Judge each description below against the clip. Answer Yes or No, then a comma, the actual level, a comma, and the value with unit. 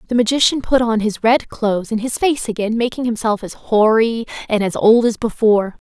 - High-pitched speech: Yes, high, 225 Hz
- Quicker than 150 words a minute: Yes, fast, 205 wpm